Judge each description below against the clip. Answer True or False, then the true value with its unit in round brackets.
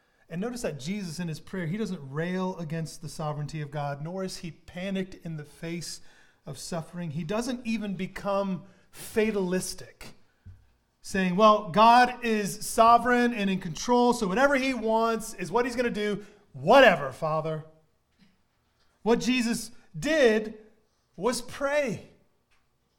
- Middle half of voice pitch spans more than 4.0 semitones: True (5.3 semitones)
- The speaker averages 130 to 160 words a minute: True (140 wpm)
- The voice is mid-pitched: False (195 Hz)